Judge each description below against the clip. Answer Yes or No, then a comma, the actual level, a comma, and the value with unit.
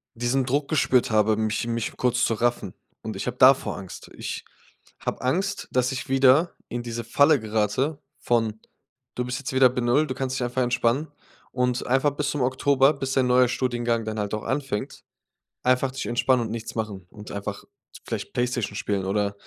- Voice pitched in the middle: No, low, 125 Hz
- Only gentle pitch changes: No, average, 3.0 semitones